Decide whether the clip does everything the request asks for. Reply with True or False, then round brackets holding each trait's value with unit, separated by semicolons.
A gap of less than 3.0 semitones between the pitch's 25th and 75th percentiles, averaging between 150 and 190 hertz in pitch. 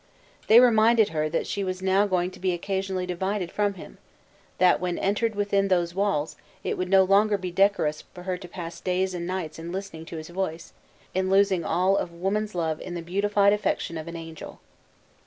True (2.4 semitones; 185 Hz)